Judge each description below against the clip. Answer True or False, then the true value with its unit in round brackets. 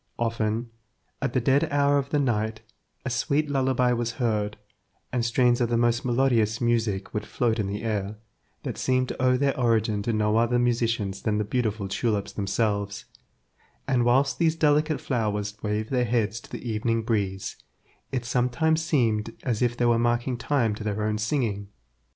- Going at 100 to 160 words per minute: False (175 wpm)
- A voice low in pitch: True (115 Hz)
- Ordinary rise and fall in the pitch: True (3.0 semitones)